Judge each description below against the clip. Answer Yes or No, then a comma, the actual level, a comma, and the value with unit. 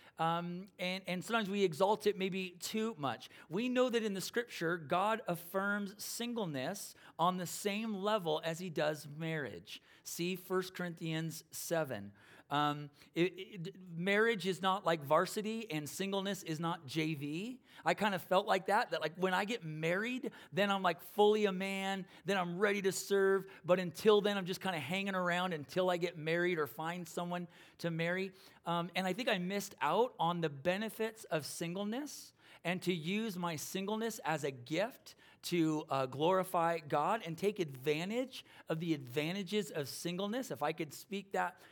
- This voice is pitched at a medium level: Yes, medium, 180 Hz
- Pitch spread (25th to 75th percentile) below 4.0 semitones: Yes, average, 3.6 semitones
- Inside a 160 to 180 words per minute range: Yes, average, 175 wpm